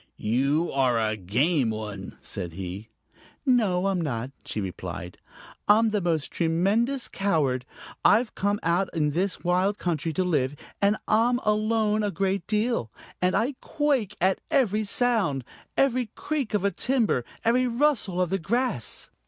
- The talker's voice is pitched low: No, high, 190 Hz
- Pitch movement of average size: No, wide, 7.7 semitones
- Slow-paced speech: No, average, 155 wpm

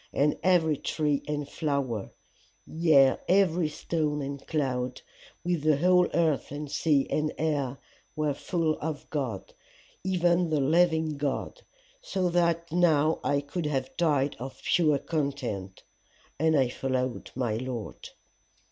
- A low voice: No, medium, 150 Hz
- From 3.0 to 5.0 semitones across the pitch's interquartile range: Yes, average, 3.3 semitones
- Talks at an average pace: No, slow, 130 wpm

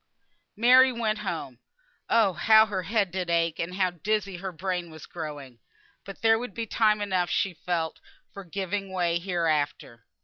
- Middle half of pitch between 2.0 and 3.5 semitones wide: No, average, 4.0 semitones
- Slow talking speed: No, average, 165 wpm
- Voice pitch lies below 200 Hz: Yes, medium, 185 Hz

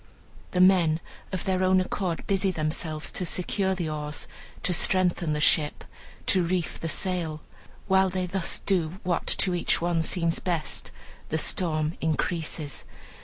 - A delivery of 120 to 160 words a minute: Yes, average, 150 wpm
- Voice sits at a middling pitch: Yes, medium, 175 Hz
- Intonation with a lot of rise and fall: No, average, 2.7 semitones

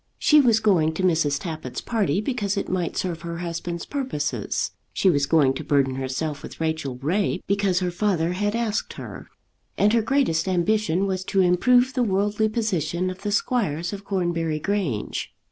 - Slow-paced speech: No, average, 175 wpm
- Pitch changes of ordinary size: Yes, average, 4.5 semitones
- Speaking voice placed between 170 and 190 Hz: Yes, medium, 185 Hz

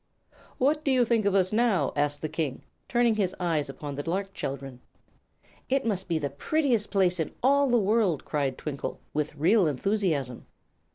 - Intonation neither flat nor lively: No, wide, 7.5 semitones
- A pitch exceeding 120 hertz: Yes, medium, 185 Hz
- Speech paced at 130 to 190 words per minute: Yes, average, 175 wpm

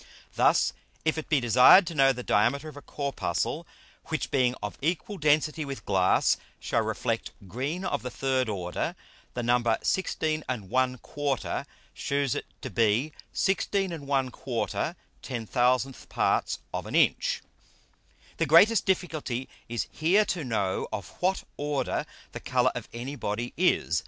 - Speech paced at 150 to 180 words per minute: No, average, 140 wpm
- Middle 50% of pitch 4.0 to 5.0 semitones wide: Yes, average, 4.4 semitones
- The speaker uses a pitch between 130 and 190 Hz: Yes, low, 135 Hz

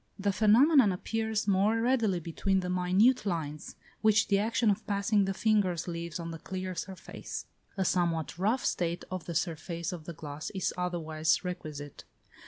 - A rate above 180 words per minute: No, average, 165 wpm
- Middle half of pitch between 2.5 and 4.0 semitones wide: Yes, average, 3.7 semitones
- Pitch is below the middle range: No, medium, 185 Hz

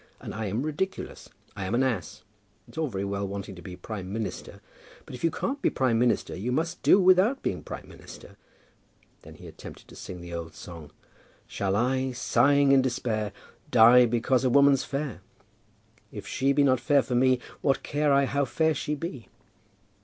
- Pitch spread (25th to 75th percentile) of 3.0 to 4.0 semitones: No, wide, 5.4 semitones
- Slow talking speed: No, average, 190 wpm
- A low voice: Yes, low, 125 Hz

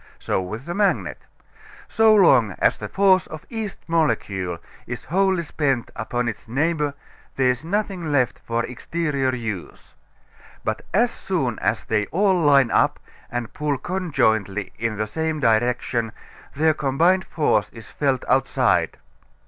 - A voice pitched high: No, low, 135 Hz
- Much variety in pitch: Yes, wide, 6.7 semitones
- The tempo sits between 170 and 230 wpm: No, average, 140 wpm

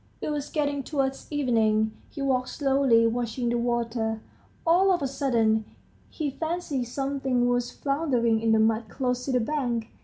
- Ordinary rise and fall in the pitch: Yes, average, 3.4 semitones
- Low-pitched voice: No, very high, 250 Hz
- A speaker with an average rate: Yes, average, 160 wpm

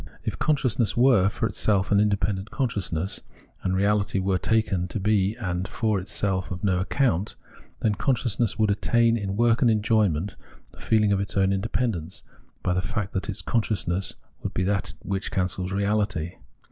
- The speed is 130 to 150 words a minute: No, average, 170 wpm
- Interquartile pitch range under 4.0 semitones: Yes, average, 2.7 semitones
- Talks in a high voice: No, low, 100 Hz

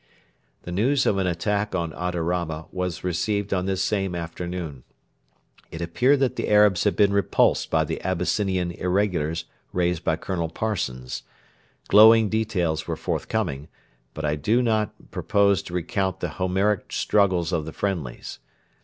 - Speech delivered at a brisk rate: No, average, 145 wpm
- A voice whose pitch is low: Yes, very low, 90 Hz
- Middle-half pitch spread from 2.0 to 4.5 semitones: Yes, average, 3.4 semitones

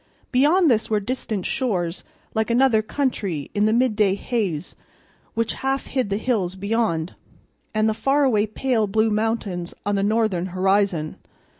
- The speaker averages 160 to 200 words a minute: No, average, 145 wpm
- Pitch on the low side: No, high, 215 Hz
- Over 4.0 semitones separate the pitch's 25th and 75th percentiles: No, average, 3.6 semitones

